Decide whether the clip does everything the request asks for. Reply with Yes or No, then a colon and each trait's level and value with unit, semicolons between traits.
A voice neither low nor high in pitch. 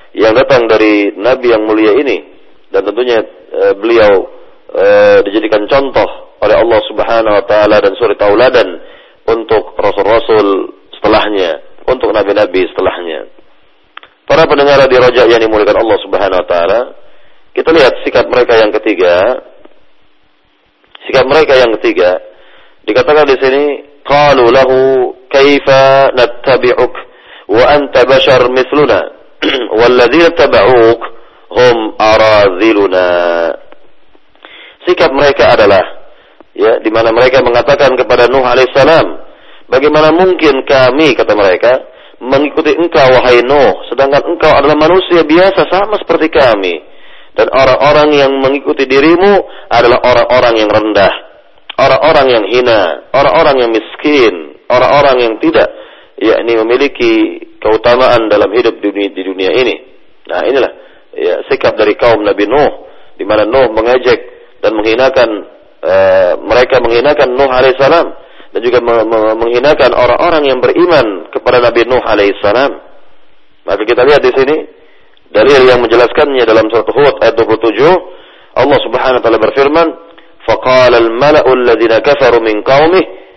Yes: medium, 145 Hz